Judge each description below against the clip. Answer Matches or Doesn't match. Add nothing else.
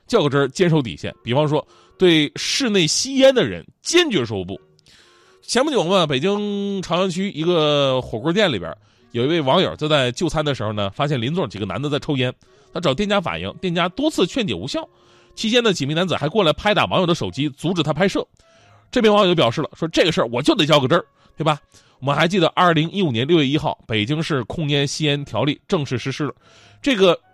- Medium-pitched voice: Matches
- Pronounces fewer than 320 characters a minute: Doesn't match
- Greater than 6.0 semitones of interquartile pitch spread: Doesn't match